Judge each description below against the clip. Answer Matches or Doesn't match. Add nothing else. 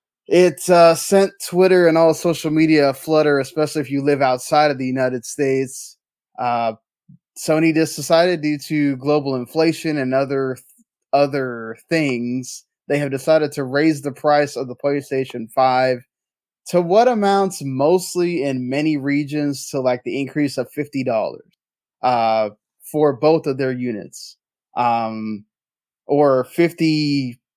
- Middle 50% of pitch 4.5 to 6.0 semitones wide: Doesn't match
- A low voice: Doesn't match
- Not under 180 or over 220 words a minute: Doesn't match